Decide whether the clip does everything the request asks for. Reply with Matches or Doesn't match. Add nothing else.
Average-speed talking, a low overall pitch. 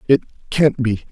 Matches